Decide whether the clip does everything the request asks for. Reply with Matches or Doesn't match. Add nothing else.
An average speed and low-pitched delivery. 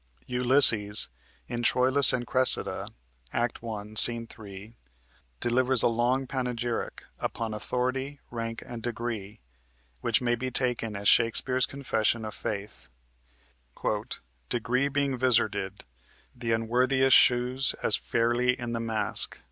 Doesn't match